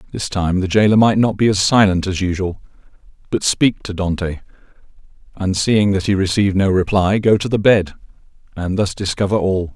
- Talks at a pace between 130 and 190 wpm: Yes, average, 185 wpm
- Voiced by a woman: No, male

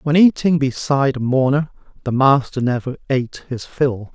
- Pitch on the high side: No, low, 135 Hz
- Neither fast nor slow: Yes, average, 160 wpm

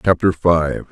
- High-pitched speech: No, very low, 85 Hz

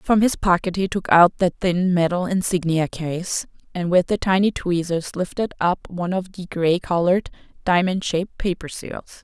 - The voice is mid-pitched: Yes, medium, 180 Hz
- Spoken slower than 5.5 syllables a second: Yes, 4.8 syllables/s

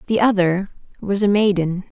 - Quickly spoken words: No, average, 150 wpm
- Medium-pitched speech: No, high, 195 Hz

